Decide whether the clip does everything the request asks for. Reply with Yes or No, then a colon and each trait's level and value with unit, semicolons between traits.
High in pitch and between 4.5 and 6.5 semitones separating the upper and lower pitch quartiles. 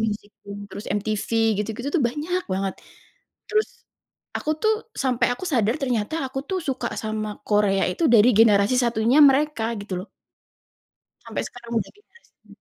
Yes: high, 235 Hz; wide, 5.4 semitones